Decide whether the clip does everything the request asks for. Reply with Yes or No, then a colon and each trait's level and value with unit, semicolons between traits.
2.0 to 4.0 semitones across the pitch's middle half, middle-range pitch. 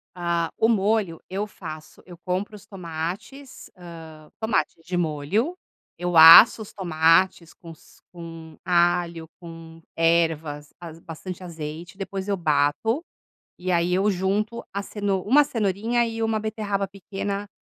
Yes: average, 3.7 semitones; medium, 180 Hz